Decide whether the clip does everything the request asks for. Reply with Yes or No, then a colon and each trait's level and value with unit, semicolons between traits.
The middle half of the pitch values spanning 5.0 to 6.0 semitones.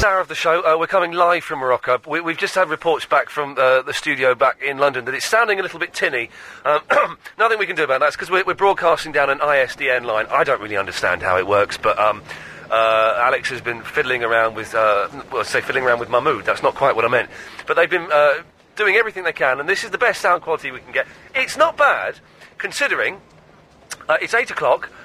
Yes: average, 5.3 semitones